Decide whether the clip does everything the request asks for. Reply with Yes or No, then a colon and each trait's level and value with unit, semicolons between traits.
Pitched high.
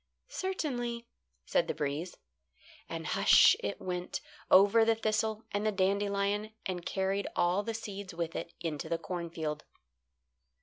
Yes: high, 200 Hz